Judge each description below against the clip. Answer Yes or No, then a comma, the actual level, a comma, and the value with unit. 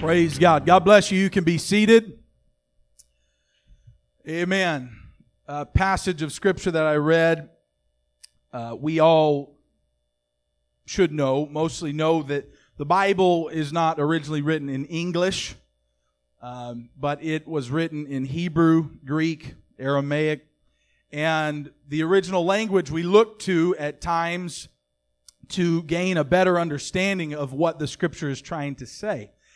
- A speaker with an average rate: No, slow, 130 wpm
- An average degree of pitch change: Yes, average, 4.7 semitones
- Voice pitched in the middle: Yes, medium, 155 Hz